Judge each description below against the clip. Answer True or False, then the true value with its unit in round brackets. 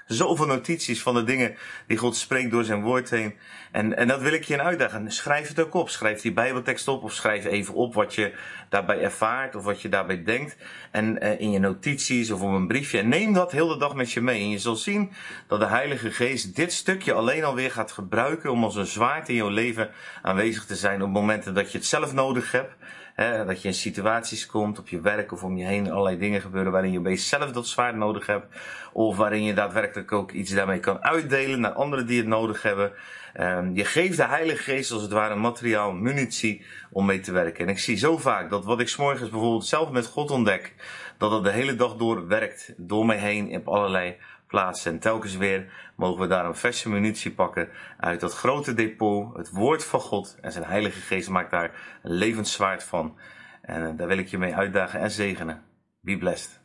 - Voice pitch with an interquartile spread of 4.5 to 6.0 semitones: False (3.8 semitones)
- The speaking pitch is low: True (110 Hz)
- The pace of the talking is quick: True (225 wpm)